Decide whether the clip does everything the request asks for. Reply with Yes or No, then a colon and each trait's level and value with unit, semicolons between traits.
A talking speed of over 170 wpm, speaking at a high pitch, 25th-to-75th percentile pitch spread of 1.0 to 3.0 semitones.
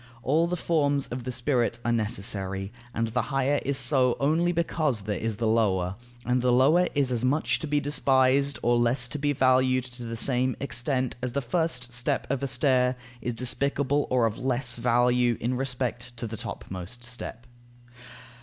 No: average, 180 wpm; low, 125 Hz; average, 2.7 semitones